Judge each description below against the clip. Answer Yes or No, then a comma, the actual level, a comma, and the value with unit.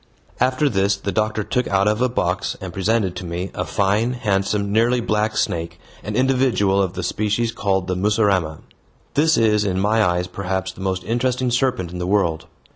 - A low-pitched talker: Yes, low, 100 Hz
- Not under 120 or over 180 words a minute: No, average, 190 wpm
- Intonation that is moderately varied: Yes, average, 3.4 semitones